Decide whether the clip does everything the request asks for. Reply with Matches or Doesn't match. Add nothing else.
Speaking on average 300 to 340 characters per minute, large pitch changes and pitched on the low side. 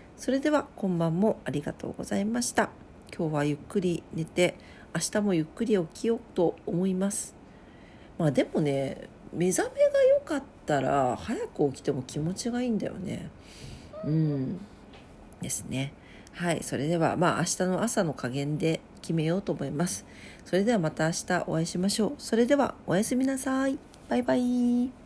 Doesn't match